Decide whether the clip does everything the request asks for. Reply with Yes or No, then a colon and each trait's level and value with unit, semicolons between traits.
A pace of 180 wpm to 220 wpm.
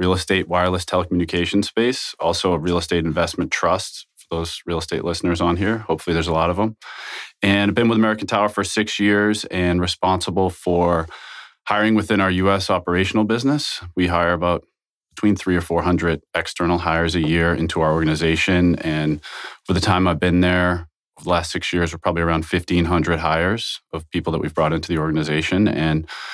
Yes: average, 185 wpm